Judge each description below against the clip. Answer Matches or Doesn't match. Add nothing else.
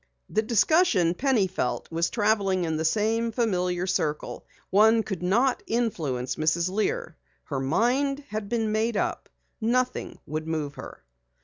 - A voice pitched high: Matches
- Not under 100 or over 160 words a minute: Matches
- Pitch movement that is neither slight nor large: Doesn't match